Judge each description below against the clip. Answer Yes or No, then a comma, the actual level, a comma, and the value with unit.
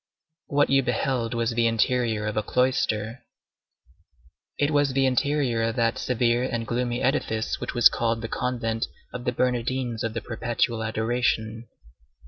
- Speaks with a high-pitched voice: No, low, 120 Hz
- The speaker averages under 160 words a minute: Yes, average, 150 wpm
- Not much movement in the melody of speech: Yes, narrow, 1.9 semitones